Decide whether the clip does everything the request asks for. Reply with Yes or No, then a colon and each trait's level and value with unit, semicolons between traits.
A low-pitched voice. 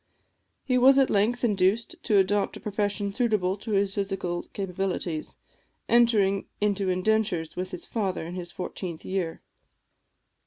No: high, 195 Hz